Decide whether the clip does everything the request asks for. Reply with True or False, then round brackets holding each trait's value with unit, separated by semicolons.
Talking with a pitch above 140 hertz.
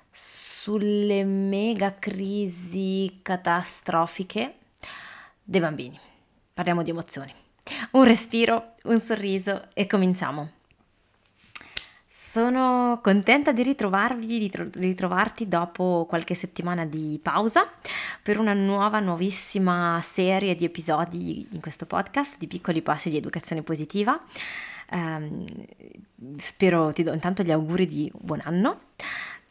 True (185 Hz)